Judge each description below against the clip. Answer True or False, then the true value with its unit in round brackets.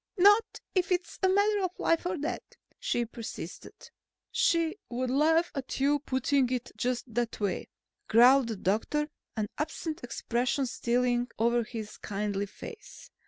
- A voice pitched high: True (255 Hz)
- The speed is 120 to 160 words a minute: True (145 wpm)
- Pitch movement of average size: False (5.7 semitones)